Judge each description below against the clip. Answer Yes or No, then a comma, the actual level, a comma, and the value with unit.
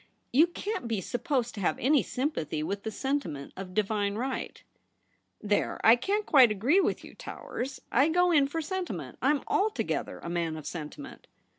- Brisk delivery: No, average, 185 wpm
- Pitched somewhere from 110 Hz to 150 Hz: No, very high, 250 Hz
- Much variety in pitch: Yes, wide, 7.2 semitones